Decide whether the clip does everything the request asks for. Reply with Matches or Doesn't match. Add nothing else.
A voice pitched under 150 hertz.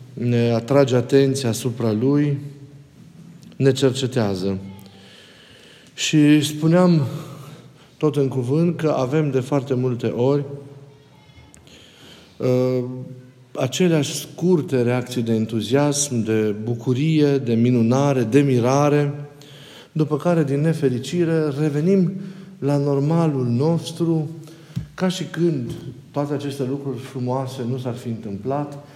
Matches